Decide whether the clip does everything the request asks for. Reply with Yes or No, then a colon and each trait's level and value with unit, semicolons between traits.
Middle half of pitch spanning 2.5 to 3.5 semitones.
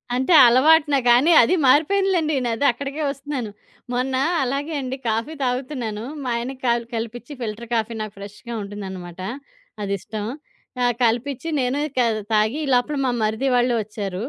No: average, 4.1 semitones